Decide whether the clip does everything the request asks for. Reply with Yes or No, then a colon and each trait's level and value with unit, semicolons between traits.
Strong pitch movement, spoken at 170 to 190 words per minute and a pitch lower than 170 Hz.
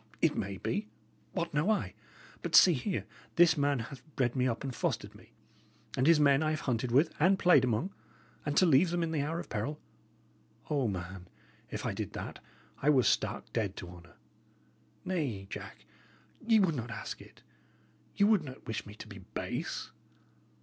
Yes: wide, 6.2 semitones; average, 185 wpm; medium, 140 Hz